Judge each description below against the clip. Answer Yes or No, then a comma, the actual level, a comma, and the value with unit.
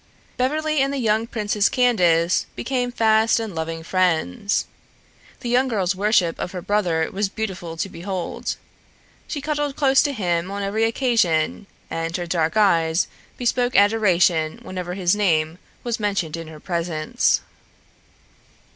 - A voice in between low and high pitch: No, high, 195 Hz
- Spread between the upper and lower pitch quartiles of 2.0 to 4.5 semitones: No, average, 5.2 semitones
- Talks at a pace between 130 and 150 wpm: Yes, average, 140 wpm